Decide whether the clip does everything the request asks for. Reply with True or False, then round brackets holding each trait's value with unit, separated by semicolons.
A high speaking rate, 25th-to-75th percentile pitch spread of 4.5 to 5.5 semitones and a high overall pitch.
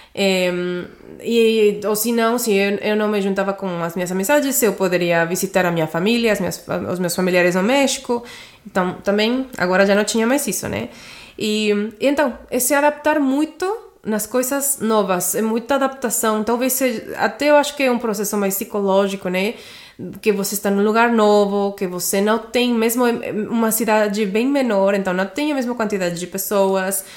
False (190 wpm; 3.8 semitones; 210 Hz)